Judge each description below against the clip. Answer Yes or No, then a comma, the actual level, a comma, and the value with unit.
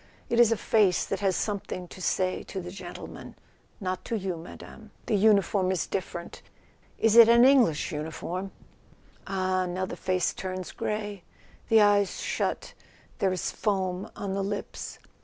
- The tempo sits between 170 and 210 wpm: No, average, 160 wpm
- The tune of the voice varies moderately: No, narrow, 2.3 semitones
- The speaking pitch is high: Yes, high, 195 Hz